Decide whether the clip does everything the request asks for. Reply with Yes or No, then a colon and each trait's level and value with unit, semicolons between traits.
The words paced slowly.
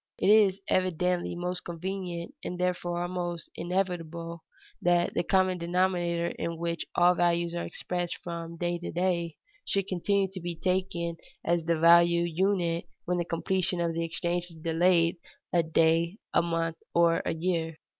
No: average, 155 wpm